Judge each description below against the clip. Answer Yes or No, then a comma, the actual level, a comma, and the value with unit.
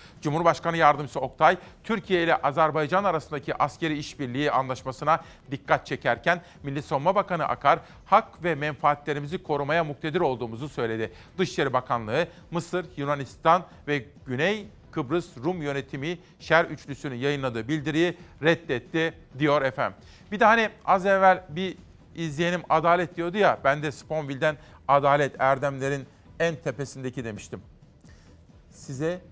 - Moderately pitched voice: Yes, medium, 155 Hz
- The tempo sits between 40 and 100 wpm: No, average, 120 wpm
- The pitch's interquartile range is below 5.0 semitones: Yes, average, 3.6 semitones